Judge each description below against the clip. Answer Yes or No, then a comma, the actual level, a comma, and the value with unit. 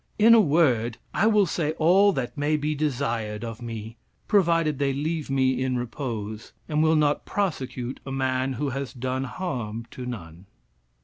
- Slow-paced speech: No, average, 170 wpm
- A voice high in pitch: No, low, 135 Hz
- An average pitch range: Yes, average, 4.5 semitones